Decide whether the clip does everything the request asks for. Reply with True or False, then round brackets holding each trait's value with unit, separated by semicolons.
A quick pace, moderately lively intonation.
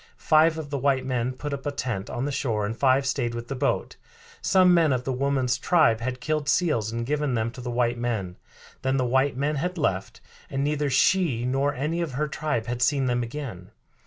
True (220 wpm; 3.5 semitones)